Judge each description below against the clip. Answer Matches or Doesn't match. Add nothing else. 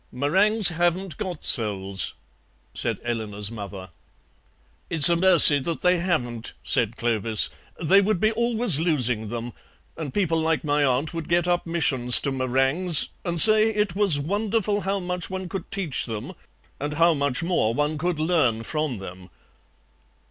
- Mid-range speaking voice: Matches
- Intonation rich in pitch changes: Matches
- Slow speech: Doesn't match